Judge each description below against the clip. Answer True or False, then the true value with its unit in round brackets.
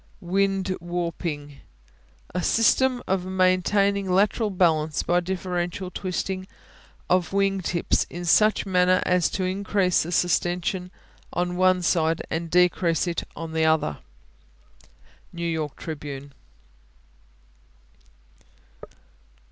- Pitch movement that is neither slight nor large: False (2.0 semitones)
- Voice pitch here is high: False (180 Hz)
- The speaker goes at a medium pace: False (105 wpm)